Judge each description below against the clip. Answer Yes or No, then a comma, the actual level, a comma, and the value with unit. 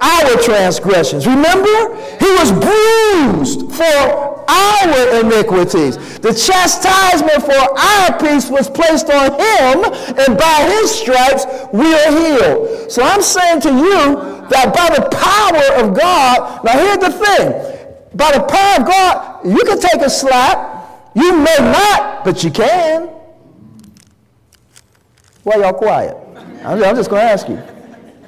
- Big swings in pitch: Yes, wide, 5.8 semitones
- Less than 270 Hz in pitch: No, very high, 320 Hz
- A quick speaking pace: No, average, 140 wpm